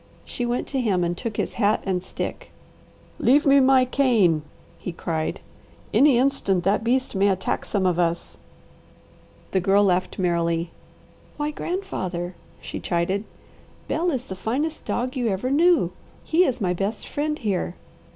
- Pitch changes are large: Yes, wide, 6.6 semitones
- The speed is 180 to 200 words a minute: No, average, 155 wpm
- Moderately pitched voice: No, high, 210 Hz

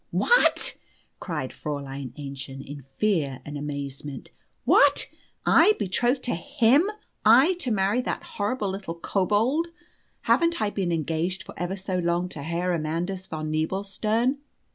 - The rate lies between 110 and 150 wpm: Yes, slow, 135 wpm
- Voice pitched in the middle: Yes, medium, 180 Hz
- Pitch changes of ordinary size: No, wide, 6.1 semitones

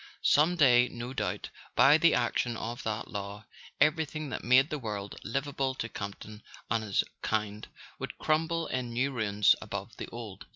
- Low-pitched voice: Yes, low, 120 Hz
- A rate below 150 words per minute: No, average, 165 wpm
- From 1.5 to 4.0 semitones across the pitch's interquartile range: No, average, 4.5 semitones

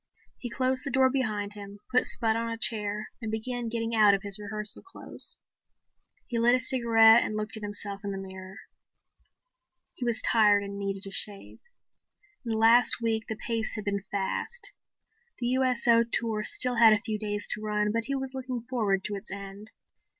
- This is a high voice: Yes, high, 220 Hz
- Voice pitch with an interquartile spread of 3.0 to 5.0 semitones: No, narrow, 2.6 semitones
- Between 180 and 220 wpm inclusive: Yes, average, 190 wpm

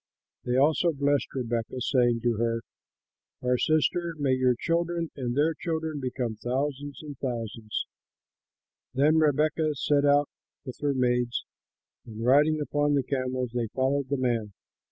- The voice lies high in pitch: No, low, 135 Hz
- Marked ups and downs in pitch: No, average, 3.2 semitones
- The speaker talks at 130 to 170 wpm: Yes, average, 140 wpm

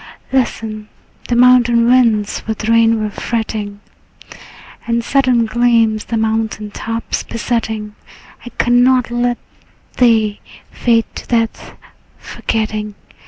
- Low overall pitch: No, high, 230 Hz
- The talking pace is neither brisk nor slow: No, slow, 105 wpm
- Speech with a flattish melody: Yes, narrow, 1.8 semitones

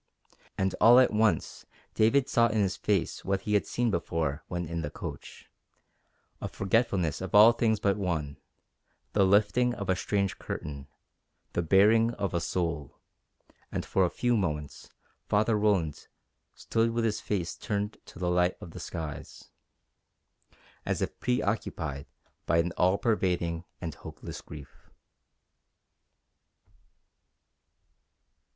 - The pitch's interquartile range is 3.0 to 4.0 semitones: No, average, 4.5 semitones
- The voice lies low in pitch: Yes, very low, 95 Hz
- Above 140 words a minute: No, slow, 135 wpm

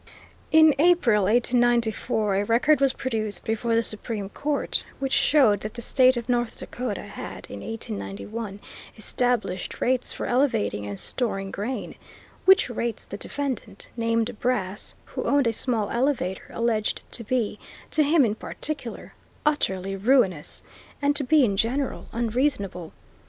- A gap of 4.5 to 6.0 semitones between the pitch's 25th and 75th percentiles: No, average, 3.8 semitones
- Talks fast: No, average, 140 wpm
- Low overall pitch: No, high, 235 Hz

